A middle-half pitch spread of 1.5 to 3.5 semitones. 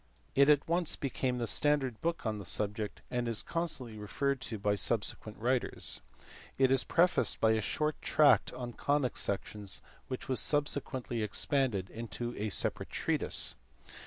No: average, 4.7 semitones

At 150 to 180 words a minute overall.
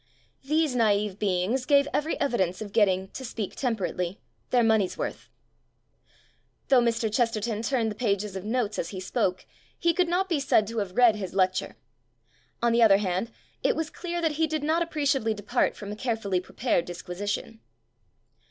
Yes: average, 175 wpm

